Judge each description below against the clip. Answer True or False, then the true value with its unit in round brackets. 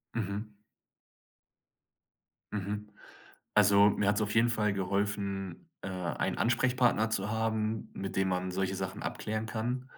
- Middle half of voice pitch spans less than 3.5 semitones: True (2.4 semitones)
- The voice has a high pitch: False (105 Hz)